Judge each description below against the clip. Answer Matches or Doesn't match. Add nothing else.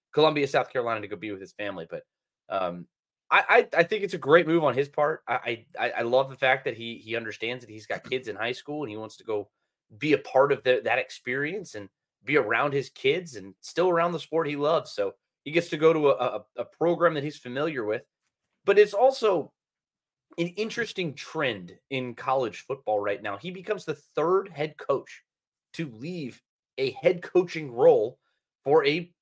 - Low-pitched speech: Doesn't match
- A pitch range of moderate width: Doesn't match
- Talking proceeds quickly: Matches